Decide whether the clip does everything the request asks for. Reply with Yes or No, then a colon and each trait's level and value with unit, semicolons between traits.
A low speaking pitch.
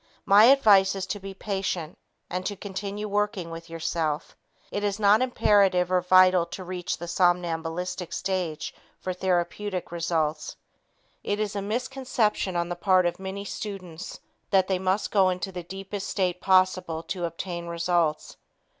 No: medium, 185 Hz